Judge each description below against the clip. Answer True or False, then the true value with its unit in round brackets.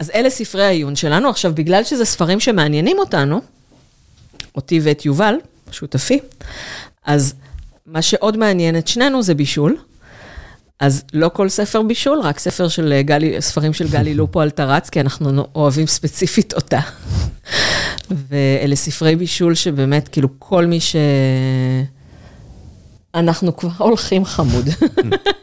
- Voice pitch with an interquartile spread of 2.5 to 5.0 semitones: False (5.4 semitones)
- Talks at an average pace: True (130 wpm)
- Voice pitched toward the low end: False (165 Hz)